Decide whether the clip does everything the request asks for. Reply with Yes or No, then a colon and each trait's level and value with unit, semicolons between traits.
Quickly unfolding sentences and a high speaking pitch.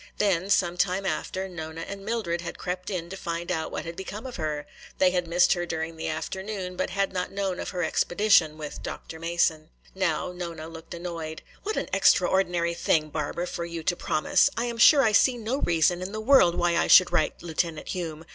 No: fast, 210 wpm; medium, 175 Hz